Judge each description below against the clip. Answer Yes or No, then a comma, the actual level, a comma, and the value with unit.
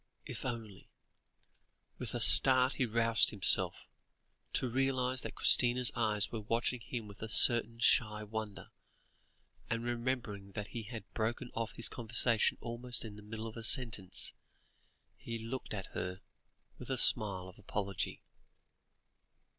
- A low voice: Yes, low, 115 Hz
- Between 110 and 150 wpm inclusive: Yes, average, 140 wpm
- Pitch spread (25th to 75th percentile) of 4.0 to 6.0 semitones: No, narrow, 2.4 semitones